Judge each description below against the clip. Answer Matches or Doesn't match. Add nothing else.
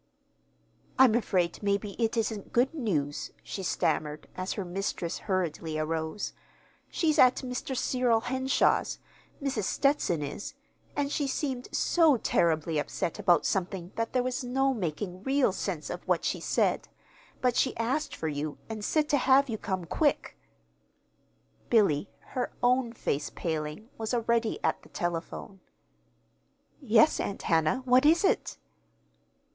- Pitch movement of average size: Doesn't match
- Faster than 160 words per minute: Doesn't match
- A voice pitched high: Matches